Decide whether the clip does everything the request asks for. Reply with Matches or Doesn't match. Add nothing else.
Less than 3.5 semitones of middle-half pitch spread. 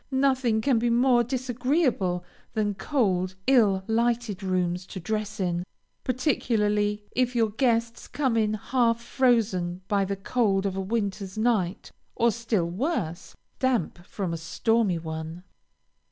Doesn't match